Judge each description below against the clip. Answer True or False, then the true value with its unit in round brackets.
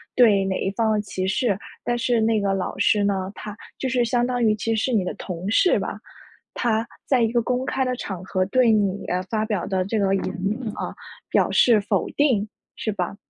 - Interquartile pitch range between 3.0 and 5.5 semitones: True (3.6 semitones)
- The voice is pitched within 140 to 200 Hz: False (215 Hz)